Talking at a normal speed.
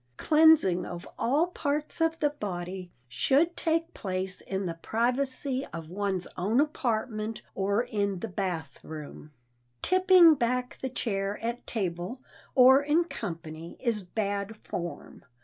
No: slow, 130 wpm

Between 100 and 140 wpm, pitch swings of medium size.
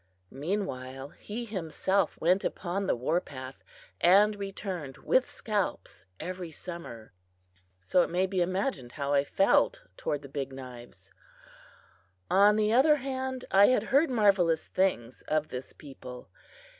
No: slow, 135 wpm; wide, 7.0 semitones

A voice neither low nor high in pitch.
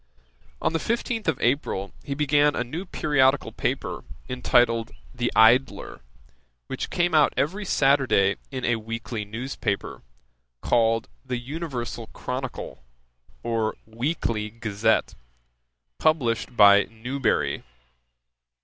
No: low, 120 Hz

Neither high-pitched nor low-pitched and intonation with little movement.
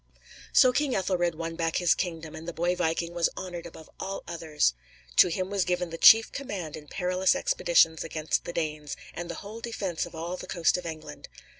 Yes: medium, 170 Hz; narrow, 2.1 semitones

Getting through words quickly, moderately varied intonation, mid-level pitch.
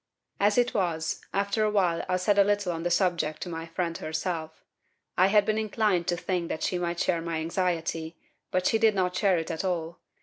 Yes: fast, 215 wpm; average, 3.2 semitones; medium, 180 Hz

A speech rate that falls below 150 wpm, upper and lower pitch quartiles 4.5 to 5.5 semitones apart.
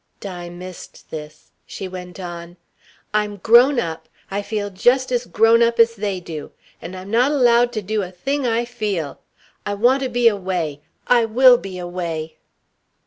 No: average, 170 wpm; average, 5.0 semitones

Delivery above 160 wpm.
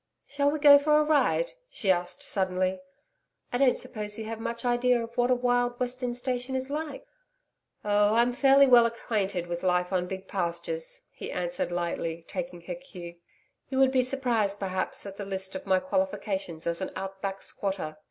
Yes: average, 185 wpm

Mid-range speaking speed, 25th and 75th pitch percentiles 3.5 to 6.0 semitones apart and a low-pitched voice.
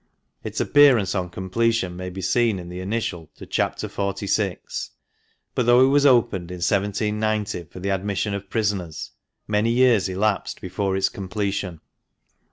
No: average, 150 wpm; average, 3.0 semitones; low, 100 Hz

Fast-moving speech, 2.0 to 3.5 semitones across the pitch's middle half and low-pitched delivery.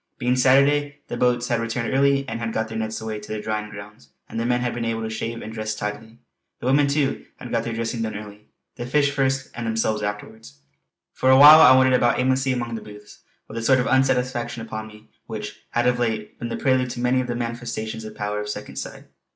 Yes: fast, 240 wpm; average, 2.8 semitones; low, 115 Hz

